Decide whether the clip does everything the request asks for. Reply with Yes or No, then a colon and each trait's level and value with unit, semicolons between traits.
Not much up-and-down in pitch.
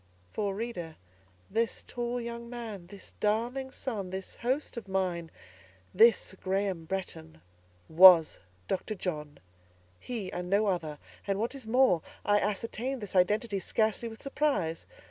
No: average, 4.7 semitones